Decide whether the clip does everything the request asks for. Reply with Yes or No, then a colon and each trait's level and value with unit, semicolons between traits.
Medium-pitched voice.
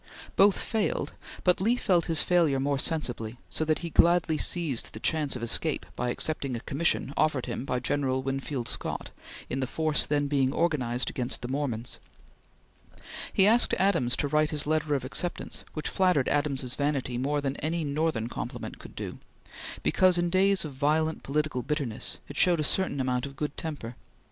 Yes: medium, 145 Hz